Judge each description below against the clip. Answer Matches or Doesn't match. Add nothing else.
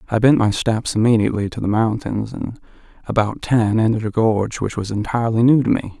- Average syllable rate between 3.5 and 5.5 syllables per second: Doesn't match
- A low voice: Matches